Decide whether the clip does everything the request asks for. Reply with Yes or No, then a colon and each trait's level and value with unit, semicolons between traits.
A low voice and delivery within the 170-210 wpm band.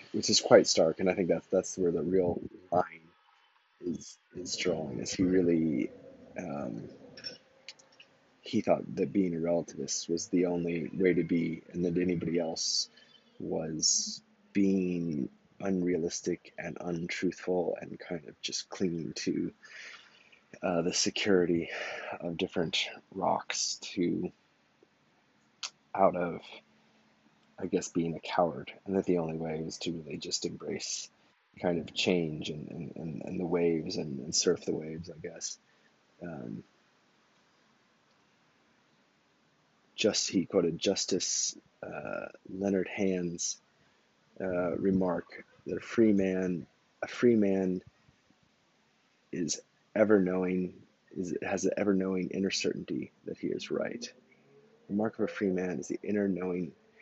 No: very low, 90 Hz; slow, 135 wpm